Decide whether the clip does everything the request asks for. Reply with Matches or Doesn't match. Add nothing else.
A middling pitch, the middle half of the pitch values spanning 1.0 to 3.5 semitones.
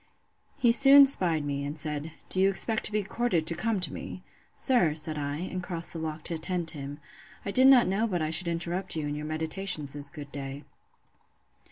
Doesn't match